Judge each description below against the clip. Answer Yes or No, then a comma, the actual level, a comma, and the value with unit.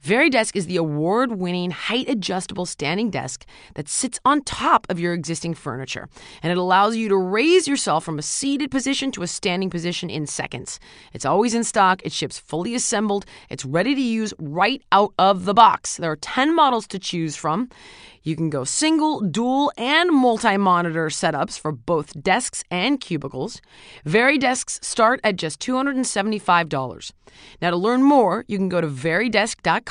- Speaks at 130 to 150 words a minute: No, average, 170 wpm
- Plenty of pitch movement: Yes, wide, 6.6 semitones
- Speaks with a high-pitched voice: Yes, high, 195 Hz